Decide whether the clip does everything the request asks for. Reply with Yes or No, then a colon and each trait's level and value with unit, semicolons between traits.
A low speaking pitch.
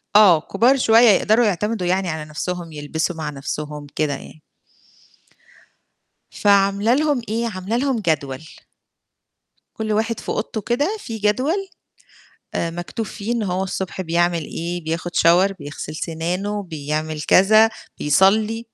No: high, 190 Hz